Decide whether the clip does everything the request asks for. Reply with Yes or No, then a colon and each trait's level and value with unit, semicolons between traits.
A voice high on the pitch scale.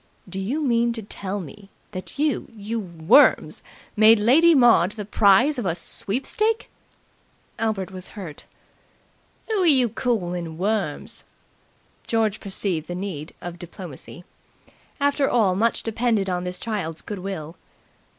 Yes: high, 205 Hz